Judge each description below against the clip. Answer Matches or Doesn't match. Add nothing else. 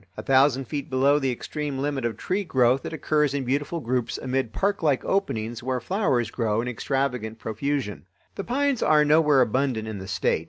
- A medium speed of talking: Matches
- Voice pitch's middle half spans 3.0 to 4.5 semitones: Matches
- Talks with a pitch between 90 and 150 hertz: Matches